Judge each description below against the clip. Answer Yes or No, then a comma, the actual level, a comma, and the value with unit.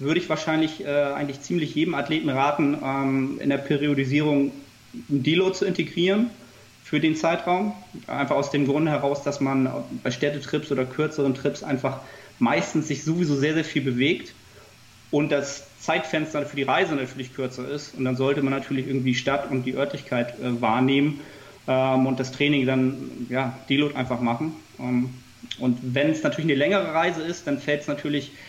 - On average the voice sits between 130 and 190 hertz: Yes, medium, 140 Hz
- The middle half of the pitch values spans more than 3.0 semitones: No, narrow, 2.4 semitones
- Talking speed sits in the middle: Yes, average, 175 wpm